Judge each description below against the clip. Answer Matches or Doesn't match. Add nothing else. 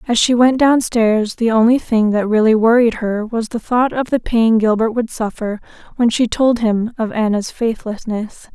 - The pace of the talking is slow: Doesn't match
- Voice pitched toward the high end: Matches